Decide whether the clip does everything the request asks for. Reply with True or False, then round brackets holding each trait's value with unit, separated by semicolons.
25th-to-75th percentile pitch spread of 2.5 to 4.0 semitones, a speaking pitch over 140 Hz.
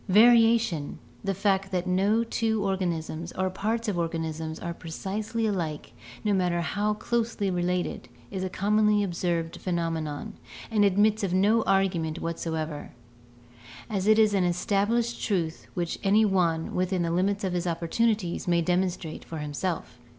True (3.6 semitones; 185 Hz)